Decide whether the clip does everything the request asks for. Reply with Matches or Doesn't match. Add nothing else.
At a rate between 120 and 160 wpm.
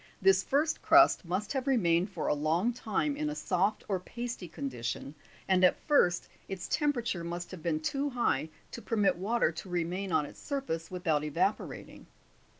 Doesn't match